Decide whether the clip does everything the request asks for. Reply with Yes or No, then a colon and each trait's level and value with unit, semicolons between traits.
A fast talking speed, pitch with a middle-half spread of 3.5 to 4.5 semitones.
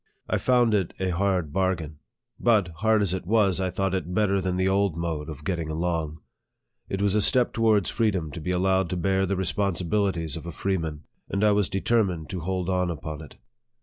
No: fast, 210 wpm; average, 2.9 semitones